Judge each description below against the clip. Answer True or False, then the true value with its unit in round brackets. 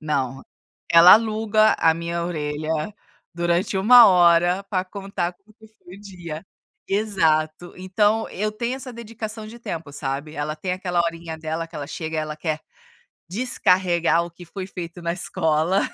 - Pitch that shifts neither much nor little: True (4.1 semitones)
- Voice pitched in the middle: True (175 Hz)